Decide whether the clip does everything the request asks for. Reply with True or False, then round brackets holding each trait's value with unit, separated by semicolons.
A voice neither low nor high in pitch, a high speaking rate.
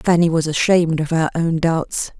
False (165 Hz; 190 wpm)